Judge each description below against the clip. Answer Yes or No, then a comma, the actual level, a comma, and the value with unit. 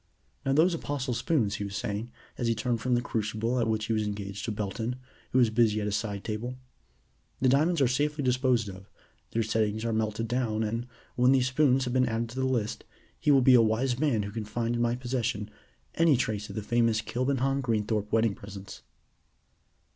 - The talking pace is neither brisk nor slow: No, fast, 210 wpm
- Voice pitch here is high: No, low, 115 Hz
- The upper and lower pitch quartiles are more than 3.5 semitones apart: No, average, 2.9 semitones